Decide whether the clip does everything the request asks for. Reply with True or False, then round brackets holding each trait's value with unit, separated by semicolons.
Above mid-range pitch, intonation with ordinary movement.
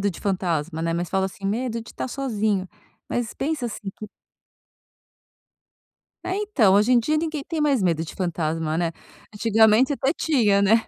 False (215 Hz; 5.9 semitones)